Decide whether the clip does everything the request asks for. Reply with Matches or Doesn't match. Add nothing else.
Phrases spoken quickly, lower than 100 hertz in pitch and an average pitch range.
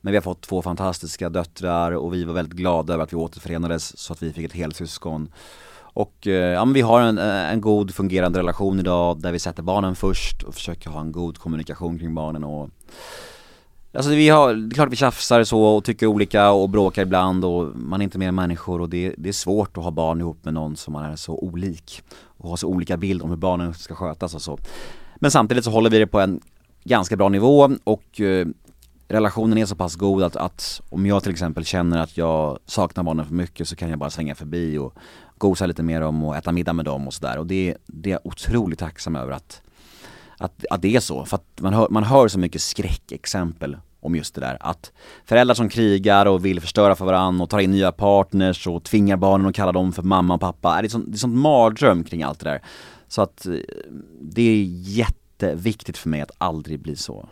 Matches